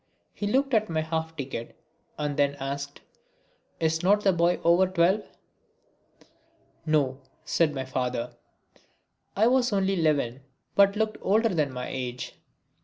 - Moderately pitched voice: Yes, medium, 160 Hz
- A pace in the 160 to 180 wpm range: No, average, 140 wpm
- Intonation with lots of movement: Yes, wide, 6.0 semitones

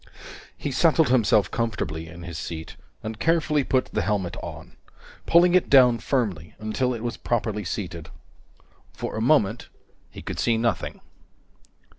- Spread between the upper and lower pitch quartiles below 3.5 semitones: No, average, 5.1 semitones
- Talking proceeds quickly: No, average, 145 wpm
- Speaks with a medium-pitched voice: No, low, 115 Hz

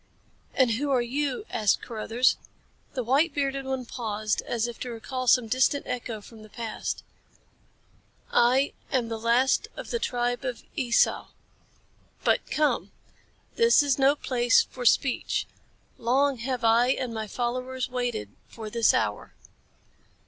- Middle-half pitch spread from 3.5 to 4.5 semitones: No, narrow, 2.5 semitones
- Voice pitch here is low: No, high, 245 Hz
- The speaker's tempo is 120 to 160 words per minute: Yes, average, 140 wpm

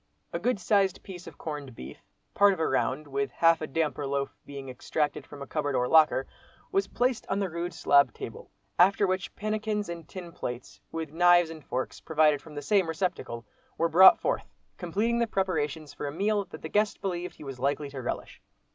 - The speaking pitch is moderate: Yes, medium, 165 Hz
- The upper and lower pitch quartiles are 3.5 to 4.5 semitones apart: No, average, 5.1 semitones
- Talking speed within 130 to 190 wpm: No, average, 200 wpm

